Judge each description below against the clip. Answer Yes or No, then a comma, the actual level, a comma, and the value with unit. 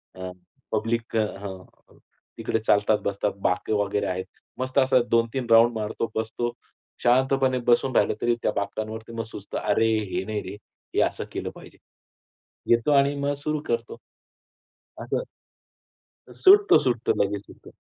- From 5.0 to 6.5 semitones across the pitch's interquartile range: No, average, 3.7 semitones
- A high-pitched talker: No, low, 115 Hz